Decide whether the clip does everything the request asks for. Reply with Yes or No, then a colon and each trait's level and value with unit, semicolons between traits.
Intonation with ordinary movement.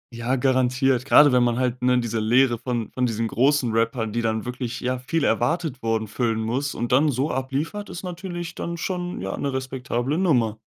Yes: average, 3.5 semitones